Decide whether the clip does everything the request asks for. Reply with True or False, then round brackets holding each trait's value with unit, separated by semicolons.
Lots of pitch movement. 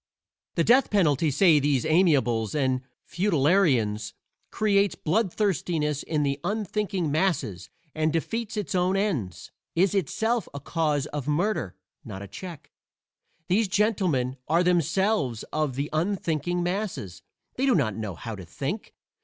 True (6.1 semitones)